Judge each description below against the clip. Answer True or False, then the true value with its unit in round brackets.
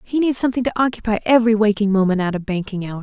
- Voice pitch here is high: True (215 Hz)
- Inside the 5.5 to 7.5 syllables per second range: True (7.3 syllables/s)